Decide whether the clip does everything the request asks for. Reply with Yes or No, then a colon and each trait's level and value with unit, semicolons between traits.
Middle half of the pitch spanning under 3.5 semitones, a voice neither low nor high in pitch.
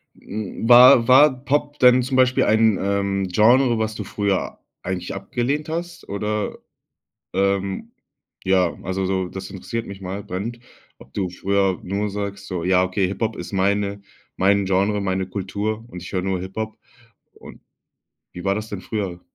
No: average, 2.8 semitones; low, 100 Hz